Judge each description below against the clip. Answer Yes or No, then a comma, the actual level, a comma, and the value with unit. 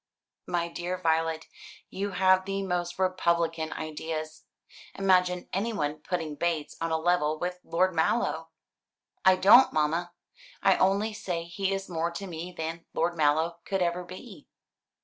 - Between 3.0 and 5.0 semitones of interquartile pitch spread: No, narrow, 2.5 semitones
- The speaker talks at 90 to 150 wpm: Yes, average, 145 wpm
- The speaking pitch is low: No, medium, 175 Hz